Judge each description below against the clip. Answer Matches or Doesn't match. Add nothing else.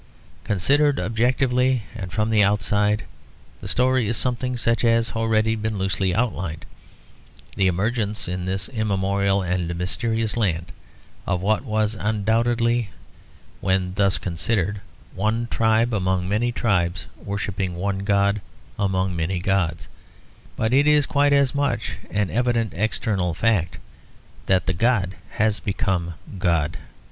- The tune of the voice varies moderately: Matches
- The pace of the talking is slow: Matches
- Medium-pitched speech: Doesn't match